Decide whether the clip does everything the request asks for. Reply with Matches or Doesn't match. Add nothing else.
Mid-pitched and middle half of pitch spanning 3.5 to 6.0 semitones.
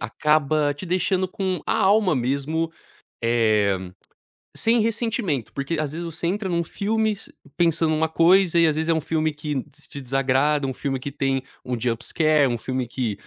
Matches